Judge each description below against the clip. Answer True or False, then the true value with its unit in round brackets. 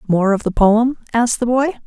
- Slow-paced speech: False (225 wpm)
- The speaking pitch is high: True (230 Hz)